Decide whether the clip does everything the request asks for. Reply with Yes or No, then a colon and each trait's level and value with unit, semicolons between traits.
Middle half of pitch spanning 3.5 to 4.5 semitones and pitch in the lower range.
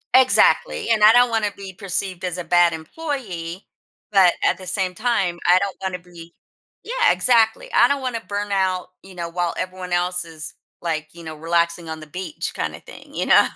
No: average, 4.1 semitones; medium, 185 Hz